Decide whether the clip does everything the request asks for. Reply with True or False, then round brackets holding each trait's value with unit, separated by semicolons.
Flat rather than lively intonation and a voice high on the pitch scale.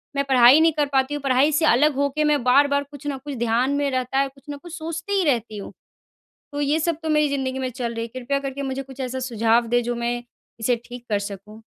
False (3.1 semitones; 265 Hz)